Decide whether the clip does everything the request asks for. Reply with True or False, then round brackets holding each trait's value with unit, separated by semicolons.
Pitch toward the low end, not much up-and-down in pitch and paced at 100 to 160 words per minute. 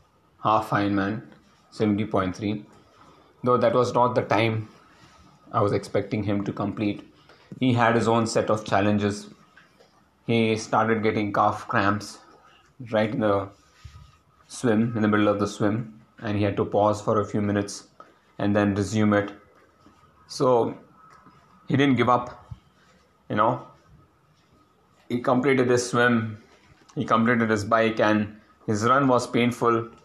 True (110 Hz; 2.3 semitones; 140 wpm)